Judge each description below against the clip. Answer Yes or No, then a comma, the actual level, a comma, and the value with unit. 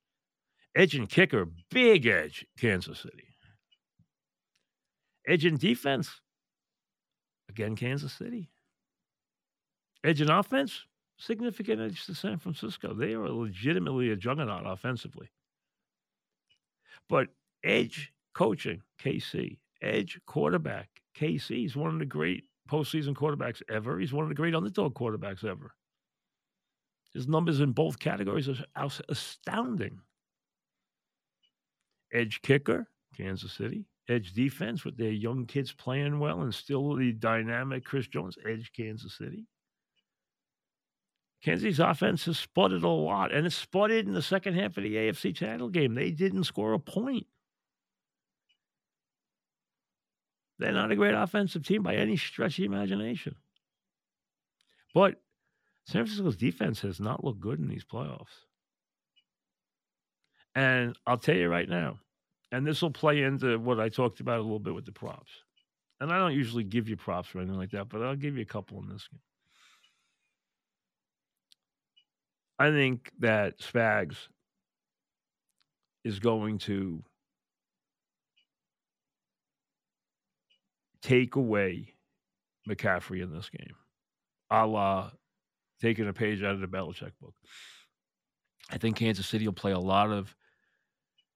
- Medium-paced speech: No, slow, 130 wpm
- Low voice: Yes, low, 125 Hz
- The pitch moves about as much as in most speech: No, wide, 6.5 semitones